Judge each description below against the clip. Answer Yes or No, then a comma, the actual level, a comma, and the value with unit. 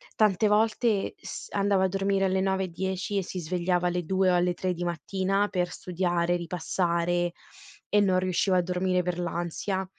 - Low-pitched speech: No, medium, 185 Hz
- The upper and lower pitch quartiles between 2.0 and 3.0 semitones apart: No, narrow, 1.6 semitones